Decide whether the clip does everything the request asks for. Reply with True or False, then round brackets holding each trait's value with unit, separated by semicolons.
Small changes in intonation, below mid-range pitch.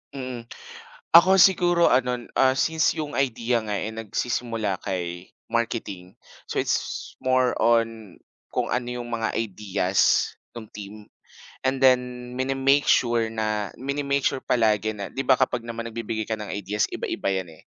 False (3.3 semitones; 115 Hz)